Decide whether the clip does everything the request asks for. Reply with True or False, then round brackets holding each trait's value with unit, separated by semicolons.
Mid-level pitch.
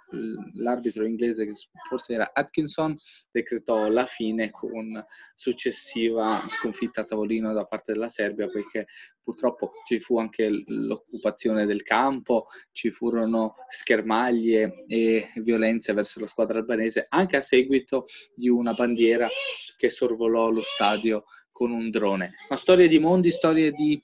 False (115 Hz)